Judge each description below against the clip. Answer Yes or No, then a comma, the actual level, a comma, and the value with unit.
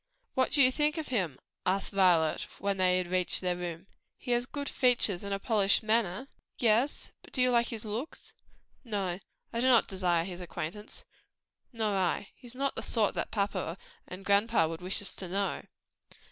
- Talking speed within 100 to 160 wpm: No, average, 190 wpm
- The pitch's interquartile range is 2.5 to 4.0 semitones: No, average, 4.6 semitones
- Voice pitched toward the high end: Yes, high, 200 Hz